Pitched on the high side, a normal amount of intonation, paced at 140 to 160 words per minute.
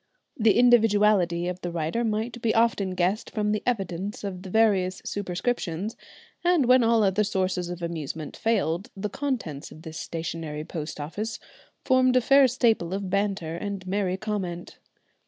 Yes: high, 200 Hz; average, 4.4 semitones; average, 155 wpm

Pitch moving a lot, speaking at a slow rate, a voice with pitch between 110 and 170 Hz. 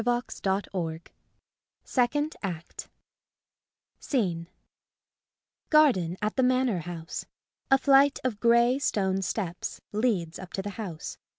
No: wide, 6.3 semitones; slow, 115 wpm; high, 210 Hz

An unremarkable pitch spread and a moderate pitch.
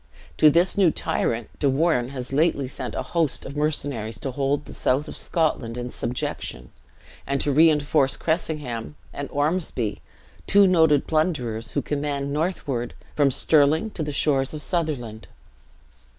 Yes: average, 3.7 semitones; medium, 145 Hz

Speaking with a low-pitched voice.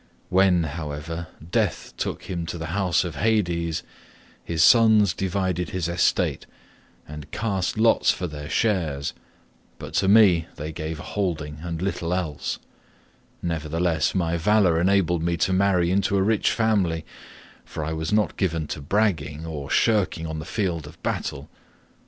Yes: very low, 85 Hz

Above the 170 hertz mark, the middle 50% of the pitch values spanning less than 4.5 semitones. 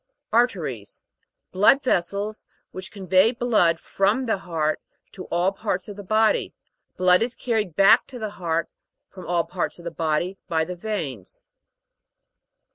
Yes: medium, 185 Hz; average, 4.1 semitones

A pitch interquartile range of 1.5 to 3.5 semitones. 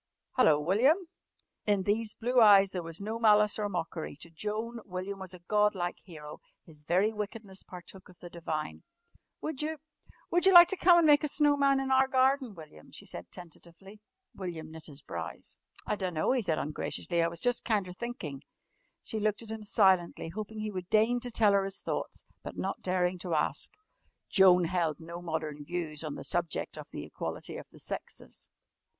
No: average, 4.7 semitones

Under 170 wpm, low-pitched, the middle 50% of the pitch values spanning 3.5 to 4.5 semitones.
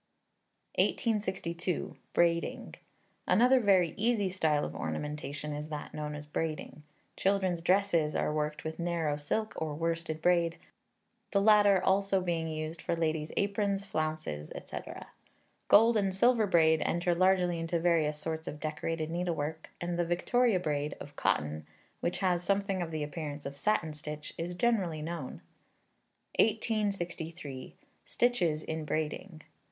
No: slow, 135 wpm; medium, 170 Hz; average, 3.8 semitones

